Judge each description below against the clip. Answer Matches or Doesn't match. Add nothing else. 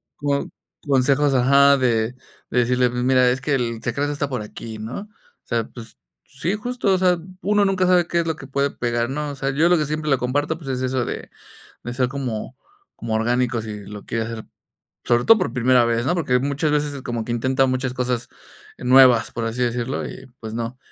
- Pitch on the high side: Doesn't match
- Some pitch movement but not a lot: Matches